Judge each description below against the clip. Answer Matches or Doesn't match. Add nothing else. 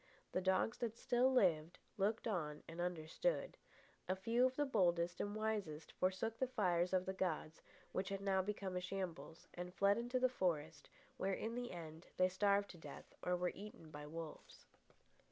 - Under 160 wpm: Doesn't match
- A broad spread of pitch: Doesn't match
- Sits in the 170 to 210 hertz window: Matches